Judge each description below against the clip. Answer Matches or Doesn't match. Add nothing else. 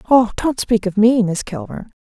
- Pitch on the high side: Matches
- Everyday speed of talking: Doesn't match